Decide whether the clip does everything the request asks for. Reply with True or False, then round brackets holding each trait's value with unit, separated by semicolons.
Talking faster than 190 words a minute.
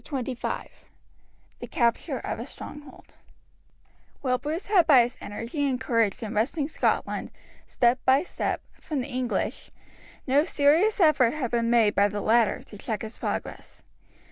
False (155 wpm)